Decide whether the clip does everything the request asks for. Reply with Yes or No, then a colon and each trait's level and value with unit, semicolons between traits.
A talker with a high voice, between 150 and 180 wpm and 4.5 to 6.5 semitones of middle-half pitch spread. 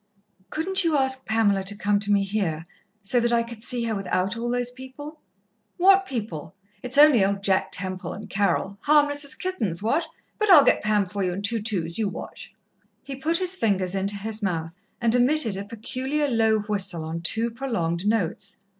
No: high, 220 Hz; average, 190 wpm; average, 5.1 semitones